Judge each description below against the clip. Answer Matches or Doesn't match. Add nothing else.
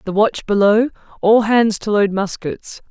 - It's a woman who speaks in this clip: Matches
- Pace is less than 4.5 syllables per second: Matches